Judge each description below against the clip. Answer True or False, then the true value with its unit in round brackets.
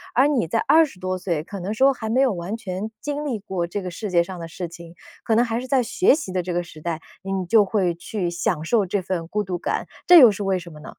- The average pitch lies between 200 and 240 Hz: False (190 Hz)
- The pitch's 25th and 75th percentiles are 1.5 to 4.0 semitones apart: False (4.8 semitones)